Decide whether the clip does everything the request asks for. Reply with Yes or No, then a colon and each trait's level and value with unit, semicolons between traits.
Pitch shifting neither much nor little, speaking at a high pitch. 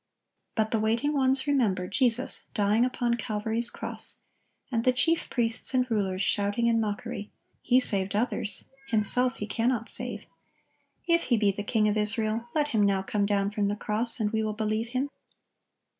Yes: average, 3.0 semitones; high, 220 Hz